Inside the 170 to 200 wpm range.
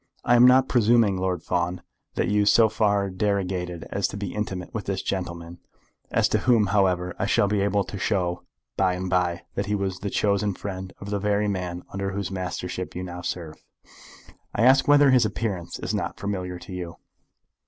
Yes: average, 195 wpm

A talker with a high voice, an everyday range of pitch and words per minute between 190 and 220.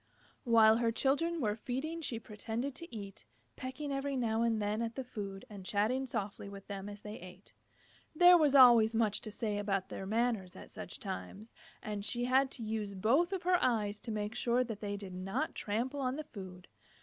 Yes: high, 225 Hz; average, 3.9 semitones; average, 200 wpm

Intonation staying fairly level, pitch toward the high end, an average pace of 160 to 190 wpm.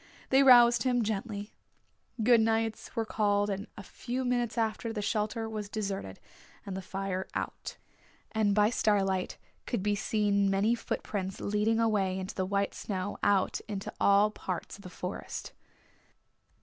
No: narrow, 2.3 semitones; high, 210 Hz; average, 150 wpm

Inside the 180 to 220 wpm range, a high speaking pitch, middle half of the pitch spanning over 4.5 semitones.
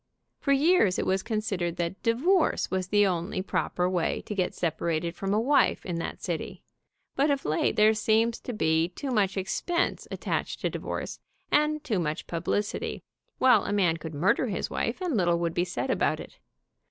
Yes: average, 190 wpm; high, 195 Hz; wide, 5.5 semitones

